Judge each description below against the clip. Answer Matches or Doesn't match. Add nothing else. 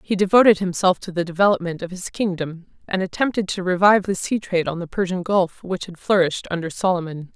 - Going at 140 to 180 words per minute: Doesn't match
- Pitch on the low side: Doesn't match